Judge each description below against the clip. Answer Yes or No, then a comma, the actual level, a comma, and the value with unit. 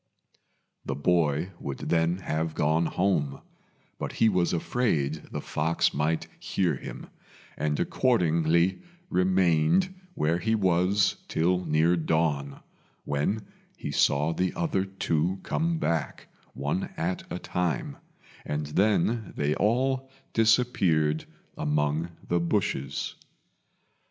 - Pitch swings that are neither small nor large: Yes, average, 3.9 semitones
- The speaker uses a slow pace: Yes, slow, 110 wpm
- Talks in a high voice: No, very low, 85 Hz